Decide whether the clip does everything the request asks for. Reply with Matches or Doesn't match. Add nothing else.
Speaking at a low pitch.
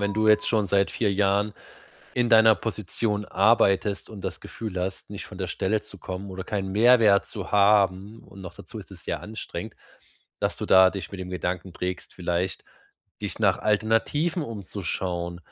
Matches